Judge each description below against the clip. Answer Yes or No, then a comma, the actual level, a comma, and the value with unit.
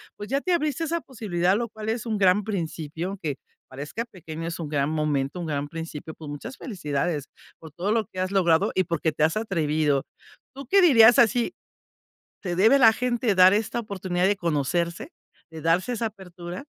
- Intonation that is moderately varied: No, wide, 5.8 semitones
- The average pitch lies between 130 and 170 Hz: No, medium, 185 Hz